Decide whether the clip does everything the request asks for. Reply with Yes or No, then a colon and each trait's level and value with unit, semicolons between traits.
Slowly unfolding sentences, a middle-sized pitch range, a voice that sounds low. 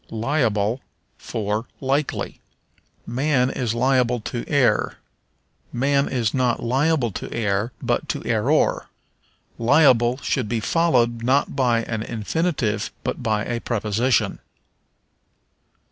Yes: slow, 110 wpm; average, 3.1 semitones; low, 120 Hz